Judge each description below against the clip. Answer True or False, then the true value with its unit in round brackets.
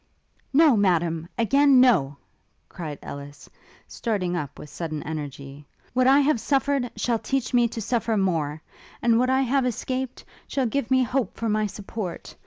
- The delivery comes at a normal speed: True (160 wpm)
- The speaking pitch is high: True (225 Hz)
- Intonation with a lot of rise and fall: True (7.8 semitones)